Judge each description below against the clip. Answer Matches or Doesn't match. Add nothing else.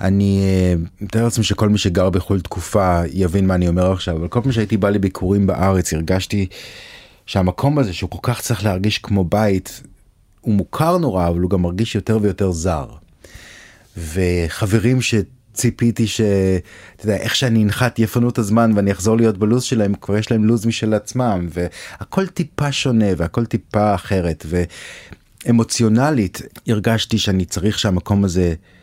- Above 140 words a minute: Matches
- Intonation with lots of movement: Doesn't match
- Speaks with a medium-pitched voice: Doesn't match